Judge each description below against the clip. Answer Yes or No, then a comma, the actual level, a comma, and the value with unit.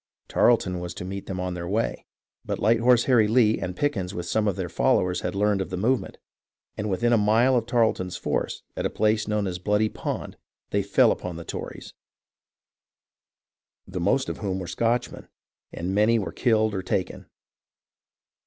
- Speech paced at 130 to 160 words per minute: No, average, 180 wpm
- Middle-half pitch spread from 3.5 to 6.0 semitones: Yes, average, 3.8 semitones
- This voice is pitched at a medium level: No, low, 105 Hz